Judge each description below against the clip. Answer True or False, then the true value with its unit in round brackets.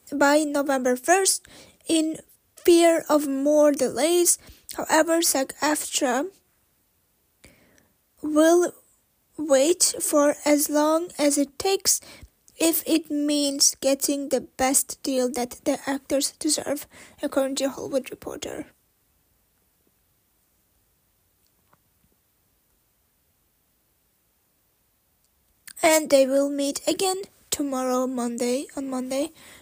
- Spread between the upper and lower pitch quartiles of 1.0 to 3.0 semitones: True (2.6 semitones)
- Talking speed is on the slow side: True (85 wpm)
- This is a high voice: True (290 Hz)